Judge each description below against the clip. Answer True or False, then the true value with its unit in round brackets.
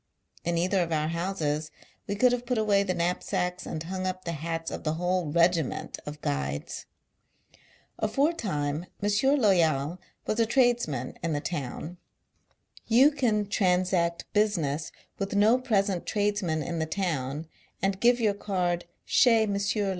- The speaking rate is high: False (155 wpm)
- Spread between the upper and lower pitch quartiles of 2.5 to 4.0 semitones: False (4.4 semitones)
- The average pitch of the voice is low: False (180 Hz)